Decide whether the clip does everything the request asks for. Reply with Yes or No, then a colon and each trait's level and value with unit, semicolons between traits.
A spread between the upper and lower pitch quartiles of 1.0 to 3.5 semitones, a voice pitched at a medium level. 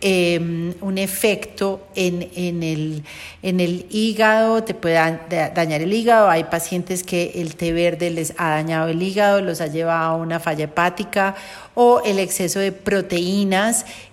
Yes: average, 2.9 semitones; medium, 180 Hz